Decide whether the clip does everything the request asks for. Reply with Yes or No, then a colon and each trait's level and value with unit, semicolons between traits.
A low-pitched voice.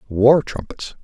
Yes: low, 125 Hz